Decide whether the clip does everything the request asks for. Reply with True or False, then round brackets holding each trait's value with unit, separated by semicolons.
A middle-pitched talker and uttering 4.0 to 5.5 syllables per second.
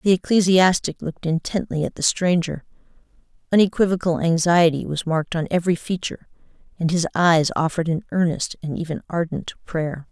False (170 Hz; 5.7 syllables/s)